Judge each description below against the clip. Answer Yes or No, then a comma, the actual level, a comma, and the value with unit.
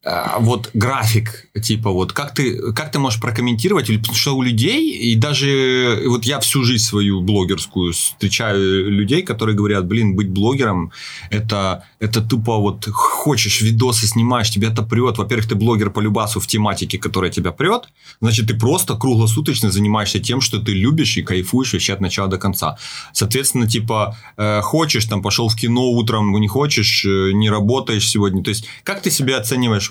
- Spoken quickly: Yes, fast, 170 wpm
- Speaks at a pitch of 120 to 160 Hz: No, low, 110 Hz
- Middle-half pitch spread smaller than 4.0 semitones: Yes, average, 3.2 semitones